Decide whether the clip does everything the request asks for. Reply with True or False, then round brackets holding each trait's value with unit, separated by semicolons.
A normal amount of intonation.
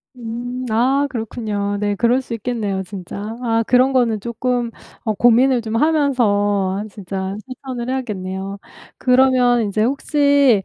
True (3.8 semitones)